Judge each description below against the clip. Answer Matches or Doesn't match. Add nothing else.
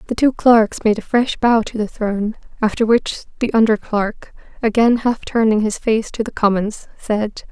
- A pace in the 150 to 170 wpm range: Doesn't match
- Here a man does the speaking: Doesn't match